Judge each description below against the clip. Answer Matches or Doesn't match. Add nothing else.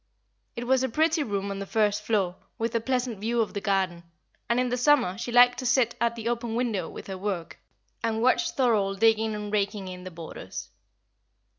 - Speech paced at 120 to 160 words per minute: Doesn't match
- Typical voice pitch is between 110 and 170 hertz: Doesn't match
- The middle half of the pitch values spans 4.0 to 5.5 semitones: Doesn't match